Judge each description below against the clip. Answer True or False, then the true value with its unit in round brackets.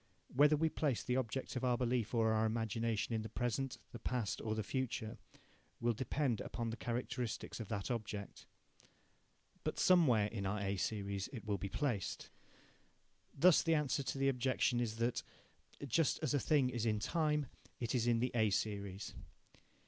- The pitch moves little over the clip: False (3.3 semitones)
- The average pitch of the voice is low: True (120 Hz)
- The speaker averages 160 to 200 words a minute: True (175 wpm)